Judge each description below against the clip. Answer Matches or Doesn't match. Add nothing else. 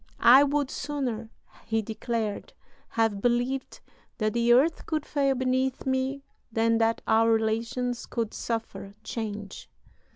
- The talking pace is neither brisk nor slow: Doesn't match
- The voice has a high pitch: Matches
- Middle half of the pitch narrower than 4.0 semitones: Matches